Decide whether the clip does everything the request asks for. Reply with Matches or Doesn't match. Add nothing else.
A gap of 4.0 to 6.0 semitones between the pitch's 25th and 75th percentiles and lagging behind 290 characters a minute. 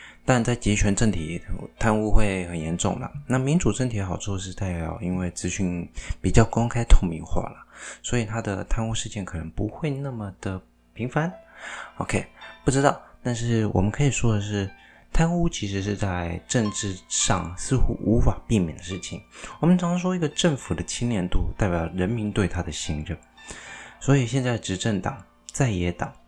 Matches